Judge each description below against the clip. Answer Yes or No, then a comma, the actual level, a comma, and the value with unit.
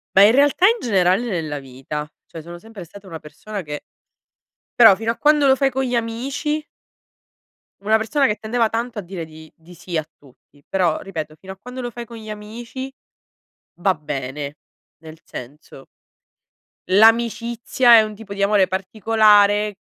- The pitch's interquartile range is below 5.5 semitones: No, wide, 6.0 semitones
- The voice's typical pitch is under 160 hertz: No, high, 205 Hz